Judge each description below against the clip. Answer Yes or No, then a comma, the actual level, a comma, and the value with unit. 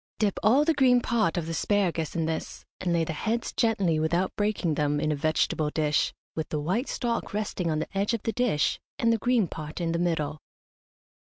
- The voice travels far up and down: Yes, wide, 6.0 semitones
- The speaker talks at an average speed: No, fast, 215 wpm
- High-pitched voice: No, medium, 175 Hz